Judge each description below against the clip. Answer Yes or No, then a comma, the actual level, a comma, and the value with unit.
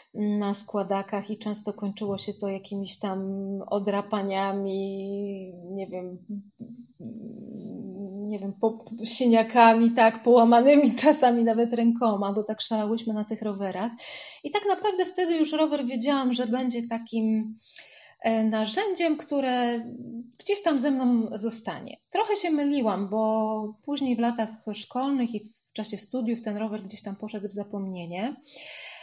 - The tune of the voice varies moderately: Yes, average, 3.2 semitones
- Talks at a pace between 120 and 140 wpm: Yes, average, 130 wpm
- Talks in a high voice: Yes, high, 225 Hz